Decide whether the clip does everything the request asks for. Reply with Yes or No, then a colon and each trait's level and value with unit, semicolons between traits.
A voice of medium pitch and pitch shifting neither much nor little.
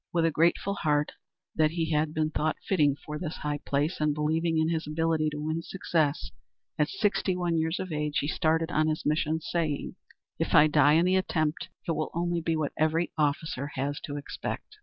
No: medium, 155 Hz; narrow, 1.7 semitones